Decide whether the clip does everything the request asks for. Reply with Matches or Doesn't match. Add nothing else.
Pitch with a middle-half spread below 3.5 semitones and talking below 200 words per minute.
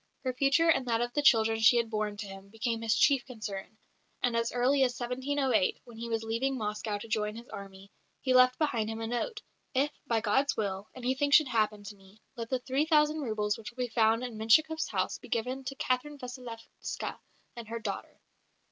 Doesn't match